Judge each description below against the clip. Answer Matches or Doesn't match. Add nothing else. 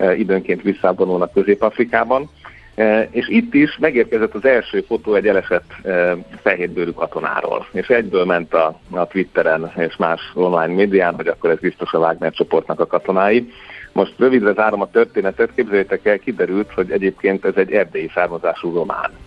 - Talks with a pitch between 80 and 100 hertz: Doesn't match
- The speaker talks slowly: Doesn't match